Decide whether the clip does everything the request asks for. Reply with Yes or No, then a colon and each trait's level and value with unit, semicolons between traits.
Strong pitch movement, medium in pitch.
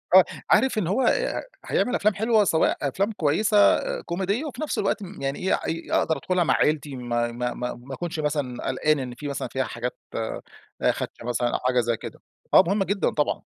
Yes: wide, 7.9 semitones; medium, 155 Hz